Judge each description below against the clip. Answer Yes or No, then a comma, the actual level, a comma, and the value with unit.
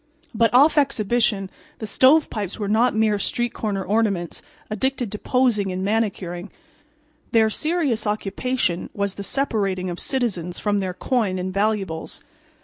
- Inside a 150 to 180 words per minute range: No, average, 140 wpm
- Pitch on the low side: No, high, 210 Hz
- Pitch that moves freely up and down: No, average, 3.8 semitones